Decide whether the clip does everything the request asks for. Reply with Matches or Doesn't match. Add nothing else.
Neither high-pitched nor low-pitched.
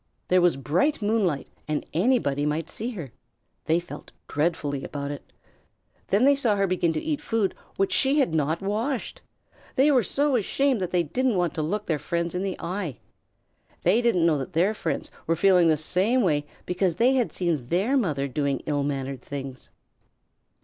Matches